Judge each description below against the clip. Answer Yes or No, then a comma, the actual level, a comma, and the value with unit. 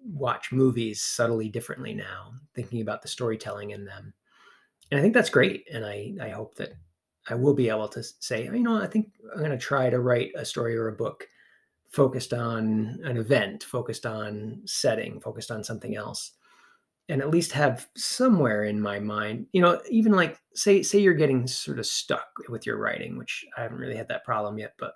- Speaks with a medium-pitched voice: No, low, 125 Hz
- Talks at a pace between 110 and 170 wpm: No, fast, 205 wpm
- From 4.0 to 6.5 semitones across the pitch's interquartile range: Yes, wide, 5.6 semitones